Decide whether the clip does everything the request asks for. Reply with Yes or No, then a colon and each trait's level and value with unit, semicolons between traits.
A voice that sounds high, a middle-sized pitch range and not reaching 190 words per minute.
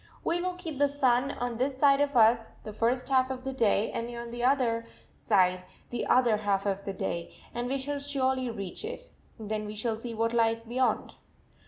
No: high, 240 Hz; average, 3.2 semitones; fast, 205 wpm